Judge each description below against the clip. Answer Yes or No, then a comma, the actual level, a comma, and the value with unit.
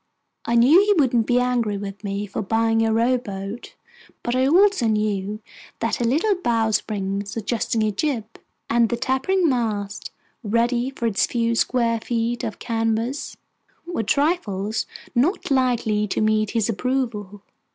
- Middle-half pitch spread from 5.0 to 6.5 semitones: No, average, 3.0 semitones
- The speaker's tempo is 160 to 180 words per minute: No, average, 145 wpm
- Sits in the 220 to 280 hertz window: Yes, high, 230 Hz